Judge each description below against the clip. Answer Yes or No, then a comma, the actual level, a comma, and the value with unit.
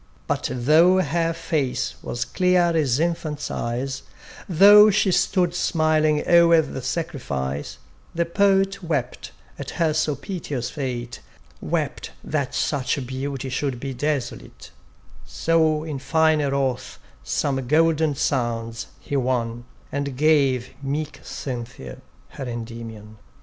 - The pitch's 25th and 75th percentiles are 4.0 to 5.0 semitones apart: Yes, average, 4.5 semitones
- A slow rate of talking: Yes, slow, 120 wpm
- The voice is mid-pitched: Yes, medium, 145 Hz